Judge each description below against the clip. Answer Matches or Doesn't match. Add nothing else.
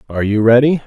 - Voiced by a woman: Doesn't match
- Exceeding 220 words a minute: Doesn't match